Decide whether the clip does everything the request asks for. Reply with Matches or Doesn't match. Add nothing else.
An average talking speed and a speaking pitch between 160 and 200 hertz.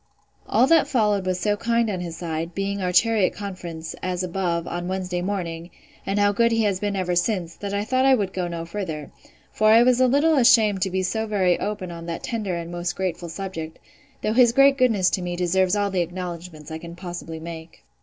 Doesn't match